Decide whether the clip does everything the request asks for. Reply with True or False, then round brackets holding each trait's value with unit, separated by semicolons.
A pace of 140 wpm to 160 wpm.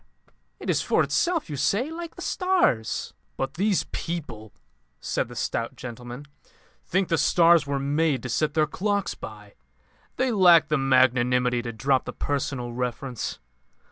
True (150 wpm)